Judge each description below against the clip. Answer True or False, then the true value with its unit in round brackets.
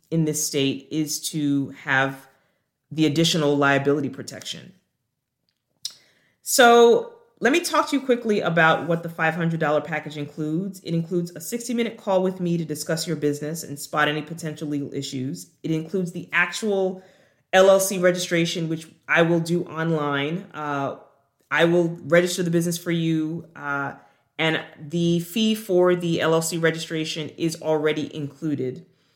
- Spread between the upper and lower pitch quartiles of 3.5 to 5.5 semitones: False (2.8 semitones)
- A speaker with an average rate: True (145 wpm)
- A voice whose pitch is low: False (160 Hz)